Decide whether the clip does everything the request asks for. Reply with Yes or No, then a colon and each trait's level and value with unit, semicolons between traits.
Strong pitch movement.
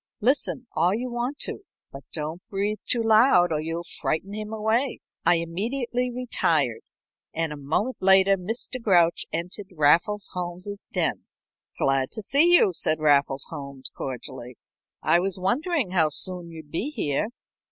Yes: wide, 6.0 semitones